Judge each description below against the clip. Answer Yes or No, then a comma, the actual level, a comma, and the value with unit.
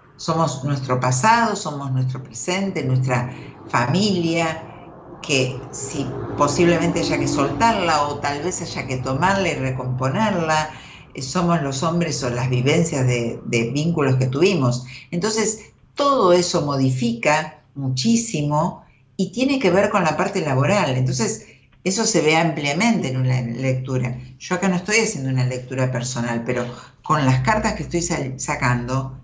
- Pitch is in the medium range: Yes, medium, 145 Hz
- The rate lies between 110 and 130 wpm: No, average, 145 wpm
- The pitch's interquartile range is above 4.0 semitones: Yes, average, 5.1 semitones